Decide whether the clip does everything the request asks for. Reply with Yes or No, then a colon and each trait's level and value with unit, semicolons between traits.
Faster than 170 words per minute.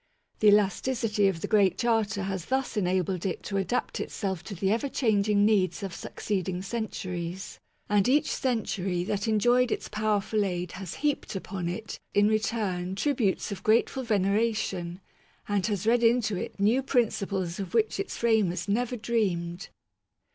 No: average, 160 wpm